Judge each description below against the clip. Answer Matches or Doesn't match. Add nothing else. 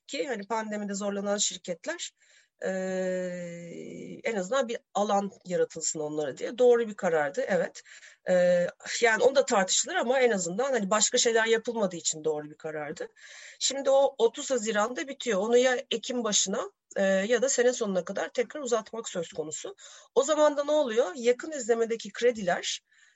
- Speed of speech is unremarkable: Doesn't match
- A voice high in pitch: Matches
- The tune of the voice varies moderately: Doesn't match